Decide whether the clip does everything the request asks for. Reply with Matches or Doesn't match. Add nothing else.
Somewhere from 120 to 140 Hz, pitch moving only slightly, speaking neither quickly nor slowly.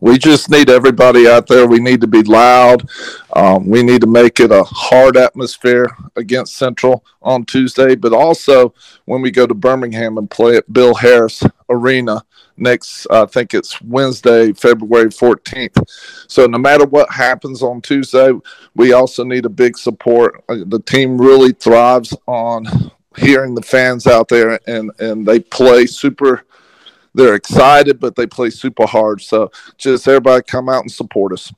Matches